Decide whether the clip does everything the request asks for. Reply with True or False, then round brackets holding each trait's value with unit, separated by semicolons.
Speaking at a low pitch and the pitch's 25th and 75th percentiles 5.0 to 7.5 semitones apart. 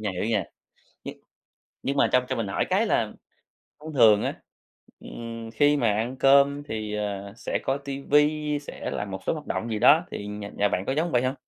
True (120 Hz; 5.4 semitones)